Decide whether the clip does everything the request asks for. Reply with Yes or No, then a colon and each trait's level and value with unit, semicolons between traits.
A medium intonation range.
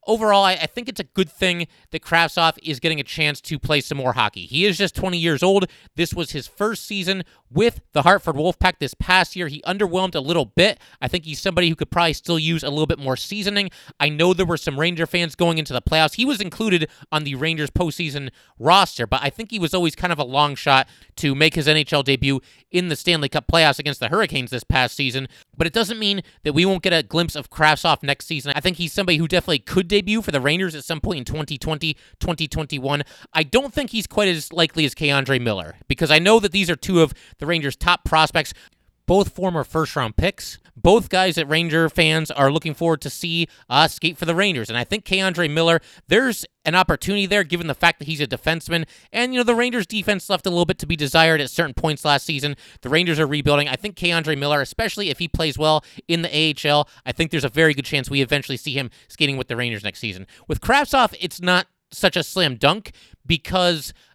Yes: average, 3.9 semitones